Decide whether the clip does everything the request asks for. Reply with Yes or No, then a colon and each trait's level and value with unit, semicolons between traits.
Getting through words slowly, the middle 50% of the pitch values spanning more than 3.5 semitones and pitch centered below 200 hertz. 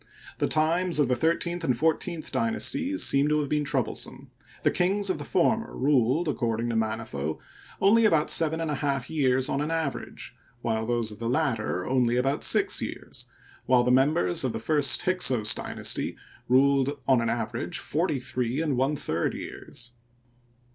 No: average, 170 wpm; average, 5.1 semitones; low, 135 Hz